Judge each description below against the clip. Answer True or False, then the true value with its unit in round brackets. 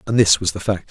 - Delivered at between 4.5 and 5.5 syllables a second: False (6.5 syllables/s)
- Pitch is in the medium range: False (95 Hz)